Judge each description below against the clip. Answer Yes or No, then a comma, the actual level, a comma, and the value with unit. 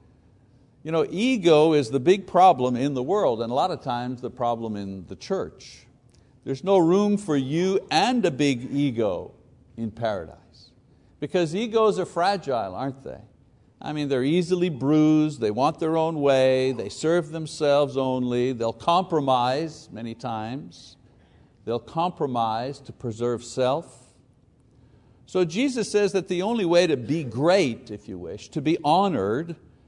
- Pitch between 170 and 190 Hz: No, medium, 140 Hz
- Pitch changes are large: Yes, wide, 5.8 semitones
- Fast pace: No, average, 155 wpm